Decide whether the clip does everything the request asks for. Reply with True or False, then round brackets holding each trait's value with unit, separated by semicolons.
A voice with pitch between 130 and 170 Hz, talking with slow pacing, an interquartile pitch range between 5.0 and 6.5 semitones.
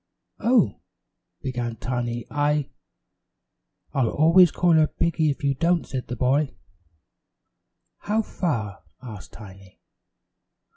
True (140 Hz; 115 wpm; 5.6 semitones)